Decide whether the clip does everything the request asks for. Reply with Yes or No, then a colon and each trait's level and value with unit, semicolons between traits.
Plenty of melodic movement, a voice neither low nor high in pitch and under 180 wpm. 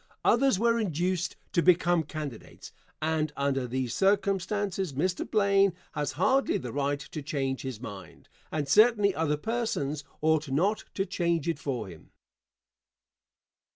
Yes: wide, 5.8 semitones; medium, 160 Hz; slow, 135 wpm